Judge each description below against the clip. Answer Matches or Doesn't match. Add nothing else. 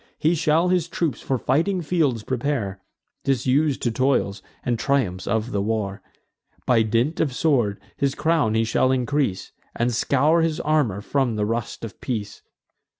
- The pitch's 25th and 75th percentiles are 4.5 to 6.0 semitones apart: Matches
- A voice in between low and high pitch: Doesn't match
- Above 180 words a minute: Doesn't match